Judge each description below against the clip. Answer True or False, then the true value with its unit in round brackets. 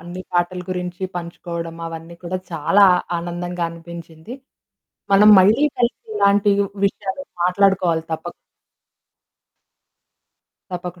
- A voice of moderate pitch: True (175 Hz)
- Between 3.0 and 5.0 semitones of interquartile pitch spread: False (2.5 semitones)